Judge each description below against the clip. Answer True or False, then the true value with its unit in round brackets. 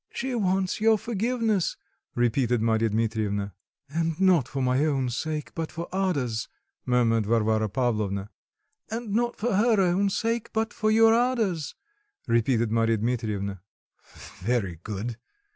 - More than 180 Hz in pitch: False (135 Hz)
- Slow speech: True (130 wpm)